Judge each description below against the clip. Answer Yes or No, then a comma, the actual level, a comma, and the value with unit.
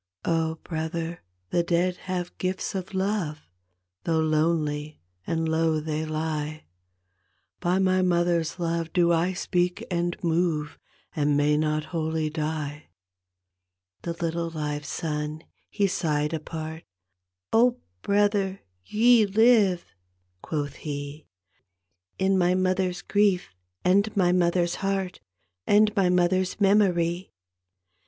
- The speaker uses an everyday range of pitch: Yes, average, 3.1 semitones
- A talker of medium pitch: Yes, medium, 170 Hz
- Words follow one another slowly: Yes, slow, 120 wpm